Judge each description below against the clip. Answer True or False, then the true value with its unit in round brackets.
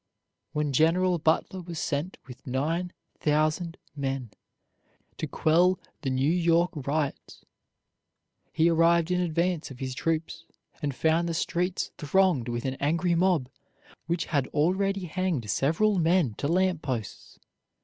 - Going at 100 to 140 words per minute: True (135 wpm)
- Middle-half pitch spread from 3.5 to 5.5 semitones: True (3.8 semitones)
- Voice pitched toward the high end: False (165 Hz)